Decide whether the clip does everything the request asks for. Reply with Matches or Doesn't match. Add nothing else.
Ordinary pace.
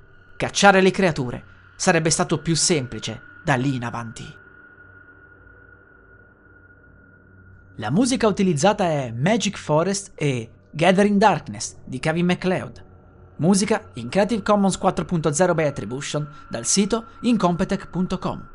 Doesn't match